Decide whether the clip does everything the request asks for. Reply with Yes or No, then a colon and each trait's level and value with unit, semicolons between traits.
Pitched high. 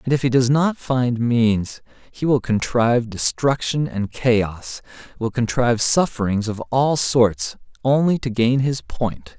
No: low, 120 Hz